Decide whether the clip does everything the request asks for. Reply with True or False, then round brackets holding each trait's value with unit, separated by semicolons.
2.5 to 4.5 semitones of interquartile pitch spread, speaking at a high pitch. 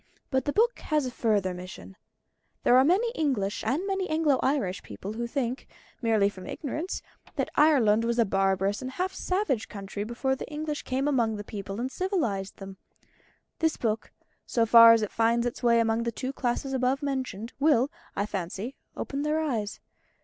False (5.3 semitones; 240 Hz)